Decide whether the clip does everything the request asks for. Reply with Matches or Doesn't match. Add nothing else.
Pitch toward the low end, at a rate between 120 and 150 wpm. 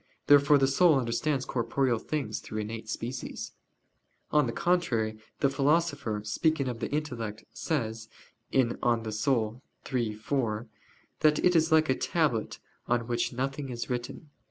Matches